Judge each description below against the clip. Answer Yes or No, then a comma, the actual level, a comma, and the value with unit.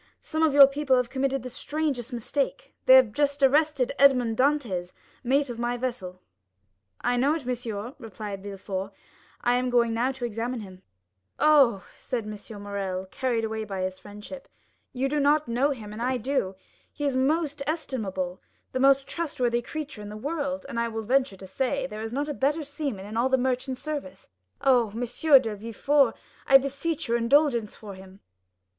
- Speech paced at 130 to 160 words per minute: No, average, 180 wpm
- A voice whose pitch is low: No, very high, 250 Hz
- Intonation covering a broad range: No, average, 4.3 semitones